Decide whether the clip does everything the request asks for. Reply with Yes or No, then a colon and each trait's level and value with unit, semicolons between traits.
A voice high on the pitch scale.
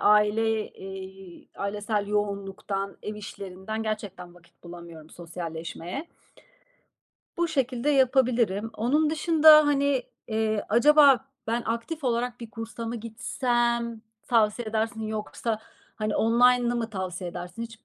Yes: high, 220 Hz